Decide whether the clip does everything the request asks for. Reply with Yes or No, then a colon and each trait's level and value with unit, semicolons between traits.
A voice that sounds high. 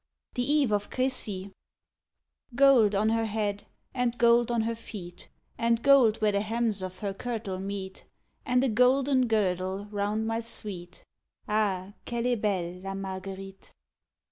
Yes: high, 215 Hz